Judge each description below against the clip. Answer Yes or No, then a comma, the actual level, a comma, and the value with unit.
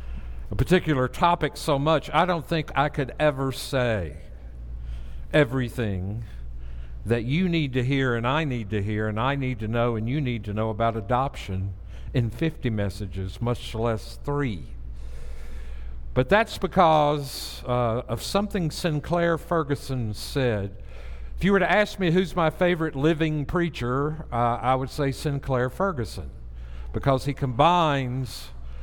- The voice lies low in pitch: Yes, low, 125 Hz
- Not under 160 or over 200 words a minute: No, average, 145 wpm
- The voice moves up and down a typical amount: No, wide, 7.3 semitones